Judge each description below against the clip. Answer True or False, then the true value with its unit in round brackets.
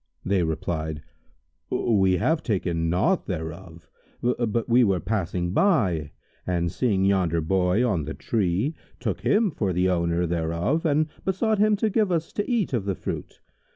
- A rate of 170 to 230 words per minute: False (155 wpm)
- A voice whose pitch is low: True (95 Hz)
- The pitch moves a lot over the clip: True (7.4 semitones)